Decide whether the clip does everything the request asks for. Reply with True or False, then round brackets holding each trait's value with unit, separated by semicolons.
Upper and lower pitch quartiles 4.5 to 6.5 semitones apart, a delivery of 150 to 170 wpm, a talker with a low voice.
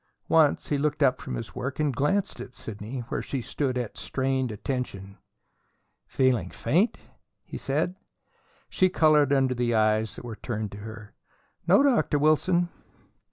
True (5.0 semitones; 155 wpm; 130 Hz)